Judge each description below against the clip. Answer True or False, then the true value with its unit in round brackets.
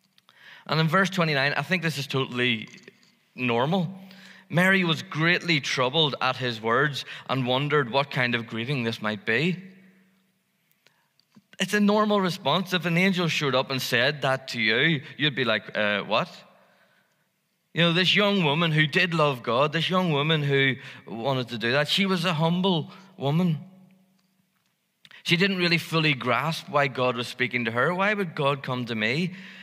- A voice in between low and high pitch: True (160 Hz)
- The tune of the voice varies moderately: False (5.9 semitones)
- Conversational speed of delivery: True (170 wpm)